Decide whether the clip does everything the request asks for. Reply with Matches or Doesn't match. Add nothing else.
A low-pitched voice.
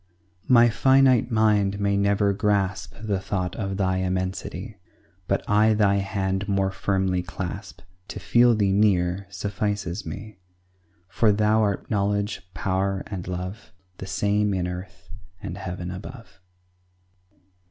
Matches